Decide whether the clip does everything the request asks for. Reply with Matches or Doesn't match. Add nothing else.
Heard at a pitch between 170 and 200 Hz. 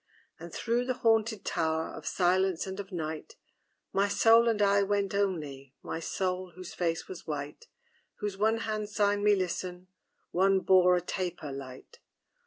Matches